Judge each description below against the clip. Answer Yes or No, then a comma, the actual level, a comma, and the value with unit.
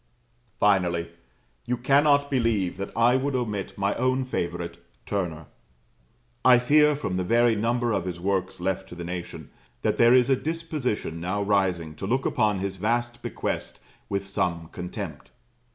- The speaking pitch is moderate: No, low, 105 Hz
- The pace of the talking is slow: No, average, 155 wpm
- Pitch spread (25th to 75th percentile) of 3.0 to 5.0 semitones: No, wide, 5.4 semitones